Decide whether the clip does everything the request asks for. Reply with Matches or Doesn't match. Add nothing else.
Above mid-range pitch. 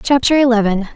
Matches